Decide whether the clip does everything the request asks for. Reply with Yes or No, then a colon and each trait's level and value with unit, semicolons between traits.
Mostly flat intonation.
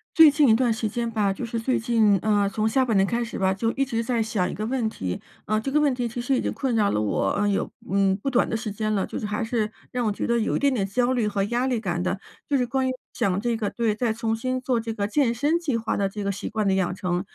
No: average, 3.4 semitones